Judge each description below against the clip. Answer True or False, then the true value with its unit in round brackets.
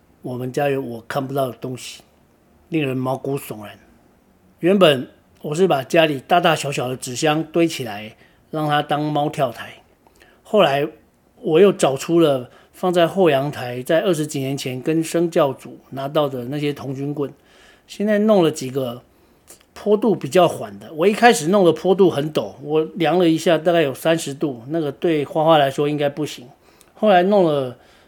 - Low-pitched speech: False (150 Hz)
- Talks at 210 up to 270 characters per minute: True (250 characters per minute)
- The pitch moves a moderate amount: True (4.0 semitones)